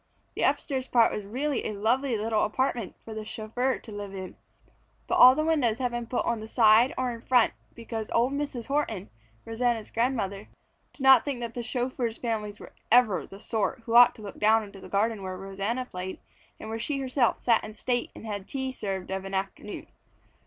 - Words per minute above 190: Yes, average, 200 wpm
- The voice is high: Yes, high, 230 Hz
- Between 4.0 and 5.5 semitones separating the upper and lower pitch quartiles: No, average, 3.2 semitones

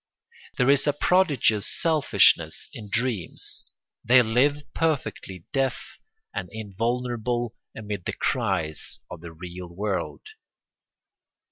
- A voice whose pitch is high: No, low, 115 Hz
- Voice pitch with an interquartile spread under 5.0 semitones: No, average, 5.3 semitones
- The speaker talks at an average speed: No, slow, 105 wpm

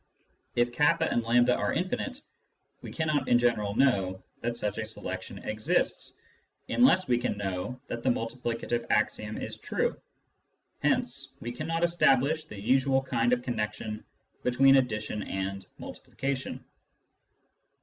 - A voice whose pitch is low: Yes, low, 120 Hz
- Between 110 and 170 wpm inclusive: Yes, slow, 135 wpm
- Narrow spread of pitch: No, average, 4.0 semitones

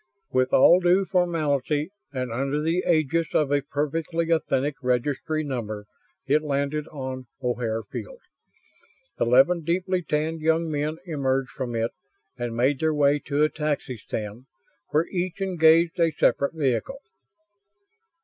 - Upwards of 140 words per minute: No, slow, 135 wpm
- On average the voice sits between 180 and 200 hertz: No, medium, 150 Hz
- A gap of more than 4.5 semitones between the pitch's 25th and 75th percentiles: No, average, 3.9 semitones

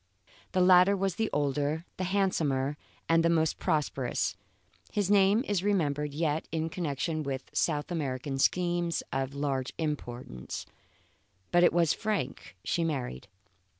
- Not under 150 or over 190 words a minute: No, slow, 135 wpm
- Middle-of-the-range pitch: Yes, medium, 160 Hz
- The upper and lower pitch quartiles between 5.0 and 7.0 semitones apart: No, average, 4.3 semitones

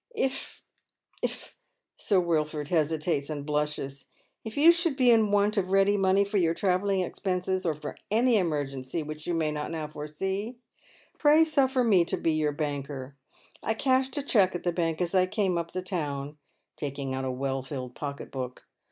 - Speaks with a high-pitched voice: No, medium, 170 Hz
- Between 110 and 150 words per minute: No, average, 195 wpm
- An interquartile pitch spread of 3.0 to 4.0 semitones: No, wide, 5.4 semitones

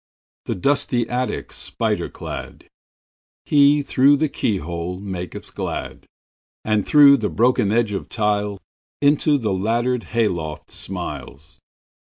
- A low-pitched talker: Yes, low, 110 Hz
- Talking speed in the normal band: No, slow, 105 wpm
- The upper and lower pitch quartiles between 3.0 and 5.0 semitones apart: No, wide, 5.6 semitones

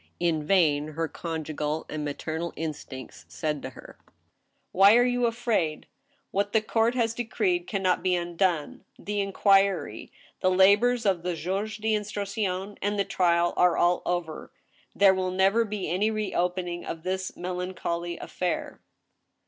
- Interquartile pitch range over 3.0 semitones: Yes, average, 3.4 semitones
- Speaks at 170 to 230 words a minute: No, average, 150 wpm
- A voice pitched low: No, medium, 185 Hz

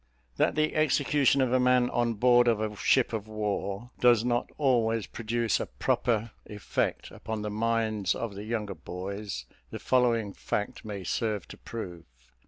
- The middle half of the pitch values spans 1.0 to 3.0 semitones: Yes, average, 2.7 semitones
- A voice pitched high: No, low, 110 Hz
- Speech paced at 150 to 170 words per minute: Yes, average, 165 wpm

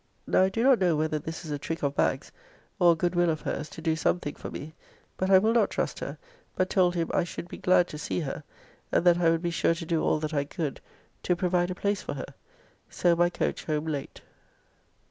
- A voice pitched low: No, medium, 170 Hz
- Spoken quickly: Yes, fast, 245 wpm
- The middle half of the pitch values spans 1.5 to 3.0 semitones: Yes, narrow, 2.4 semitones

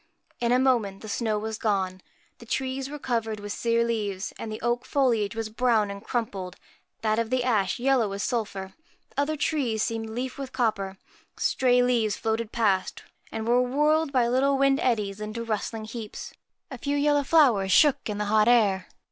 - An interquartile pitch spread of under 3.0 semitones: No, average, 3.3 semitones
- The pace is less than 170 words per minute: No, average, 180 wpm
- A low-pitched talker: No, high, 230 Hz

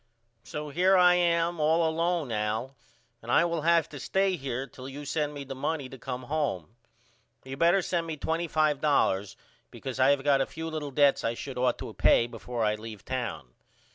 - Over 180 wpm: Yes, average, 195 wpm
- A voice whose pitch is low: No, medium, 145 Hz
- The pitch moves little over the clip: No, average, 4.6 semitones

